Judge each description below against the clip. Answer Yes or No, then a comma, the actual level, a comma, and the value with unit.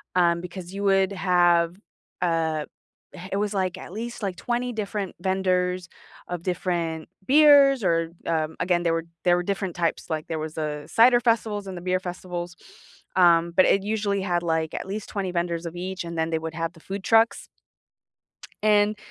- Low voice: No, medium, 180 Hz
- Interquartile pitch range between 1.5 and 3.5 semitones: Yes, average, 2.9 semitones